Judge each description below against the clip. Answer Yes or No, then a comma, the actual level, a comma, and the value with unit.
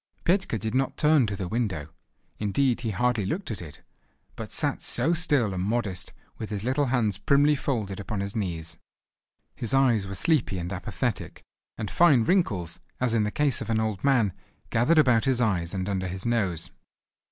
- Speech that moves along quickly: No, average, 185 wpm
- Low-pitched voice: Yes, low, 110 Hz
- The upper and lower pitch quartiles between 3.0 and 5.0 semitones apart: No, wide, 5.4 semitones